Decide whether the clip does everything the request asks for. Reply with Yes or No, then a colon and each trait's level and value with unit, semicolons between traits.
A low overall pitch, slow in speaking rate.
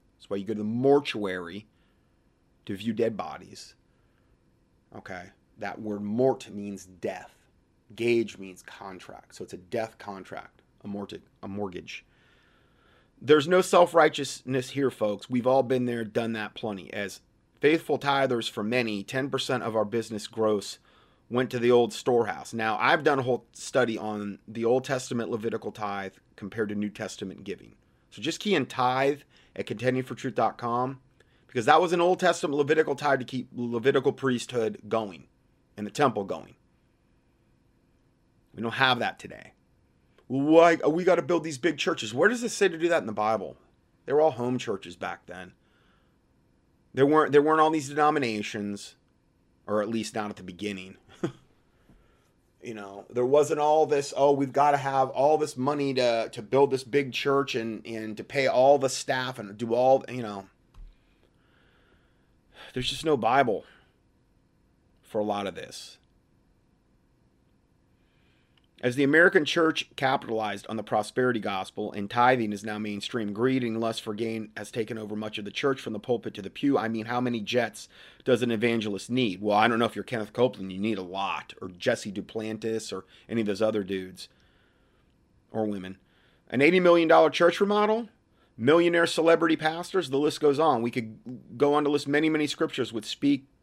No: low, 120 Hz; average, 175 wpm